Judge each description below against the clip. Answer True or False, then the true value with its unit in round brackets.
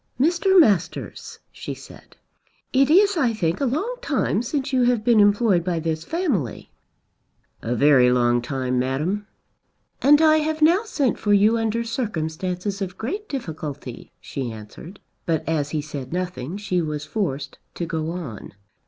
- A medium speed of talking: True (155 wpm)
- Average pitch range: False (9.0 semitones)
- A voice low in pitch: False (185 Hz)